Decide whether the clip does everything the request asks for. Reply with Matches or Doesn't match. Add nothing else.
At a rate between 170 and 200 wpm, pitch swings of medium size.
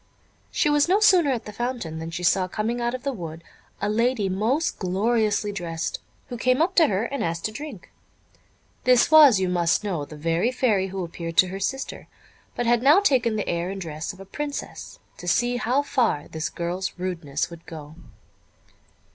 Doesn't match